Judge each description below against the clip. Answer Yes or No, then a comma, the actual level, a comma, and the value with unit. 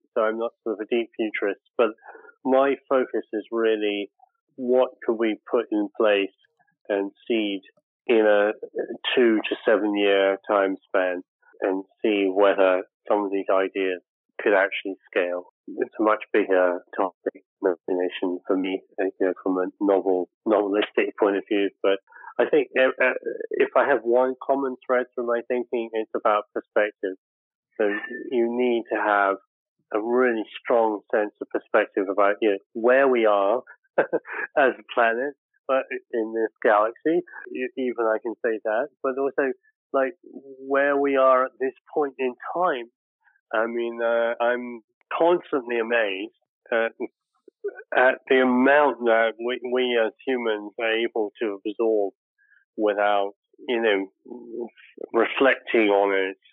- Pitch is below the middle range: Yes, low, 115 Hz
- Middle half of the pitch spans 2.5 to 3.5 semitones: No, average, 4.8 semitones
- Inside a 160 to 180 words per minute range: No, average, 145 wpm